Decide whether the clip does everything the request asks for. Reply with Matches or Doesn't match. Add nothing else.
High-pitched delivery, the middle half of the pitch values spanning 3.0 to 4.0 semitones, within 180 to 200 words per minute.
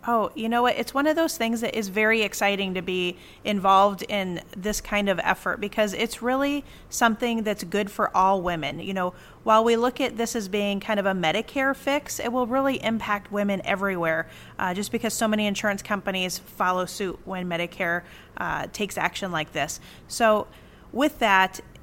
Matches